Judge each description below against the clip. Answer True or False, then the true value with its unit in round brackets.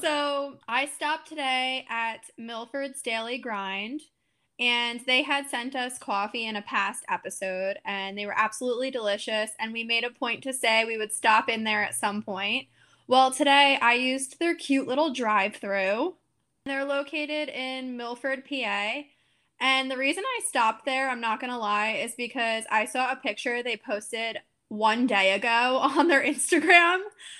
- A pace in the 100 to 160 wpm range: False (170 wpm)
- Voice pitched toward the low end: False (250 Hz)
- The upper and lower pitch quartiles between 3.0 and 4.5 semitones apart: True (3.9 semitones)